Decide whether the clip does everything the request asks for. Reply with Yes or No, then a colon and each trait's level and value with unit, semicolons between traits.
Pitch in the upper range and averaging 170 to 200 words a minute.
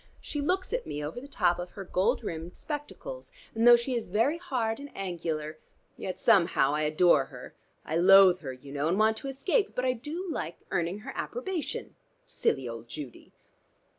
Yes: high, 195 Hz; average, 190 wpm